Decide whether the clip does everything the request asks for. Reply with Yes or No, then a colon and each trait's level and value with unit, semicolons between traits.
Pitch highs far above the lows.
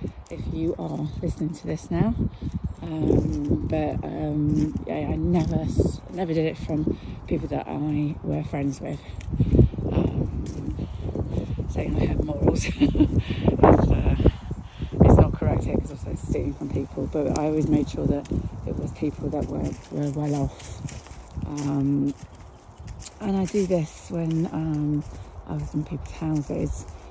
Yes: wide, 6.3 semitones